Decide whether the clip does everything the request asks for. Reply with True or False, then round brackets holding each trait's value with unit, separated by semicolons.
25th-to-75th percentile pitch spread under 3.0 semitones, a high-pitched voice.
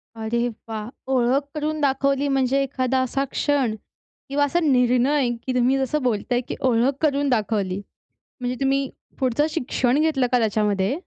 True (2.5 semitones; 260 Hz)